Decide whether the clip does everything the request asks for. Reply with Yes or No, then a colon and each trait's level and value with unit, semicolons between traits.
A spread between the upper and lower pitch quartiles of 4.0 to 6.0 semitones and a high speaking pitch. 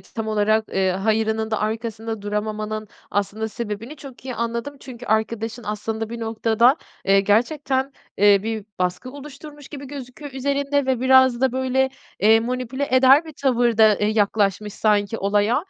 No: average, 3.6 semitones; high, 225 Hz